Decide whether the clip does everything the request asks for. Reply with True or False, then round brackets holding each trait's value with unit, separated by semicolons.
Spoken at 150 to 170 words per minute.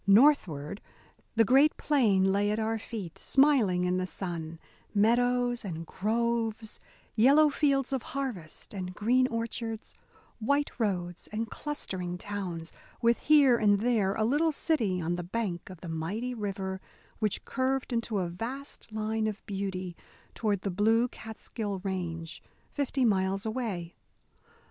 False (140 wpm)